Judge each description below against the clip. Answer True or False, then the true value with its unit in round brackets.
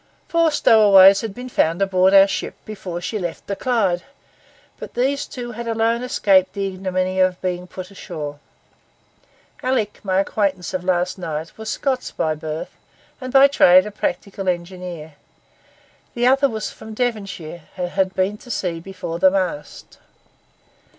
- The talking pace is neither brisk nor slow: True (155 wpm)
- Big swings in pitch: False (3.7 semitones)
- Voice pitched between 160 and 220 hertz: True (190 Hz)